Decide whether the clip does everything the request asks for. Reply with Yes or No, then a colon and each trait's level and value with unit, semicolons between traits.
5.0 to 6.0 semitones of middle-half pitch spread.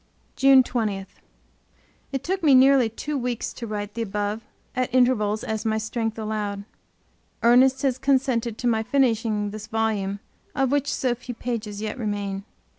No: average, 3.5 semitones